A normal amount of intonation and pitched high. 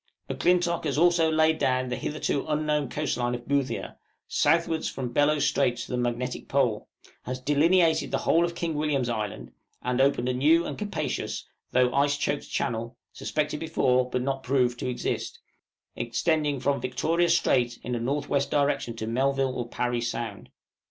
No: average, 3.7 semitones; low, 135 Hz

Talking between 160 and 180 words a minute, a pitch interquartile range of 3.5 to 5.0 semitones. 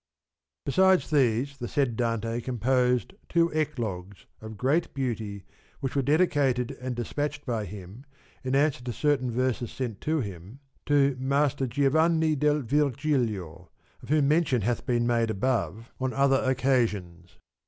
No: average, 145 wpm; average, 3.9 semitones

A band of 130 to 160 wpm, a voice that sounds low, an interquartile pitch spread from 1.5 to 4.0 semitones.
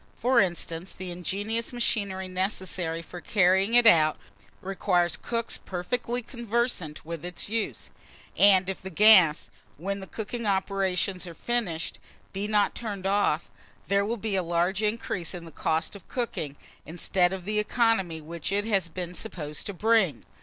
No: average, 155 wpm; high, 190 Hz; average, 3.6 semitones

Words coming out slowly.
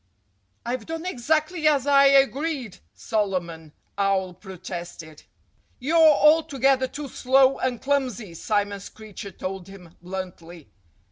Yes: slow, 110 wpm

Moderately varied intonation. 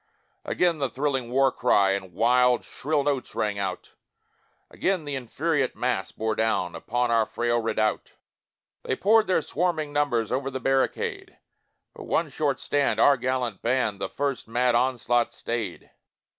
Yes: average, 3.7 semitones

